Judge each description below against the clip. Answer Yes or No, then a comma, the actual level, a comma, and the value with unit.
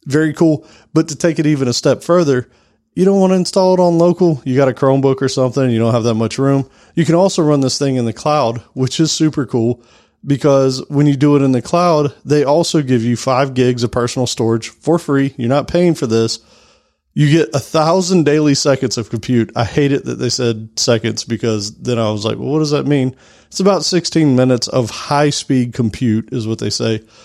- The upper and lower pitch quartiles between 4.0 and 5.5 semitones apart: Yes, average, 4.3 semitones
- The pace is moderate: No, fast, 230 wpm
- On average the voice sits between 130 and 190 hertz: Yes, low, 135 Hz